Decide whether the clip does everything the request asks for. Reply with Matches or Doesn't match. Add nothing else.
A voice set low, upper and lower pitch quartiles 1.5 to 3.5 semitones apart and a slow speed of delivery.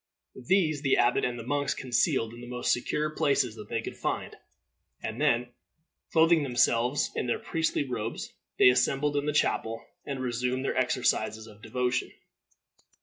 Doesn't match